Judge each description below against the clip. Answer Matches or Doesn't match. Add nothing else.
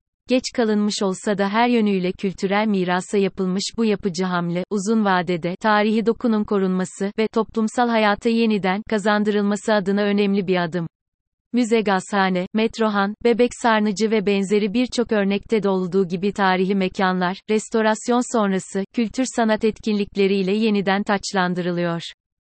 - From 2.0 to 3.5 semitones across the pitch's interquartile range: Matches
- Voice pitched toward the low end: Doesn't match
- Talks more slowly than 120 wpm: Doesn't match